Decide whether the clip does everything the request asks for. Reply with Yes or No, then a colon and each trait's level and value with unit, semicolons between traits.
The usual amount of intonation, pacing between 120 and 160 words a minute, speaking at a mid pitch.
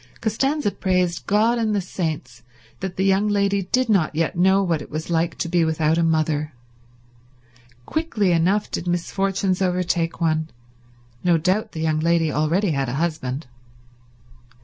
Yes: average, 3.6 semitones; average, 155 wpm; medium, 175 Hz